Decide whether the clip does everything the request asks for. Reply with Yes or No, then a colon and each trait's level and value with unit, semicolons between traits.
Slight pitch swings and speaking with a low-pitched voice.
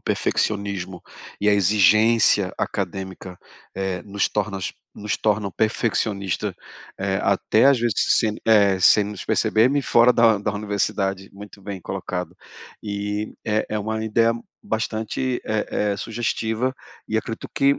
Yes: narrow, 2.0 semitones; low, 105 Hz